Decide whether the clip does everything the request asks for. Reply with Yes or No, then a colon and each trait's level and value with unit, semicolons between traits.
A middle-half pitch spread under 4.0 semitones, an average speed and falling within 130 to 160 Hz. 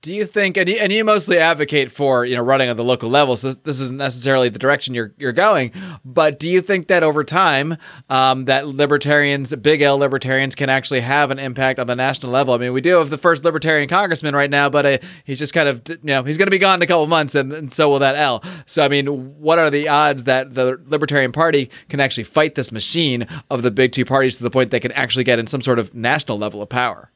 No: average, 3.0 semitones; fast, 265 wpm; medium, 140 Hz